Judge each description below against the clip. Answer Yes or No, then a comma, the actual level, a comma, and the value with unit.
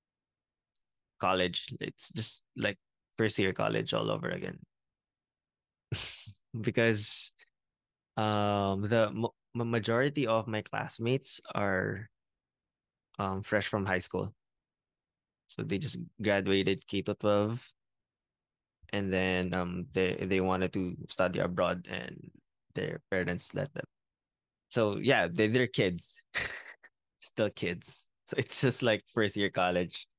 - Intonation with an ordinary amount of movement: Yes, average, 3.3 semitones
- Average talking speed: No, slow, 115 wpm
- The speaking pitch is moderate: No, low, 100 Hz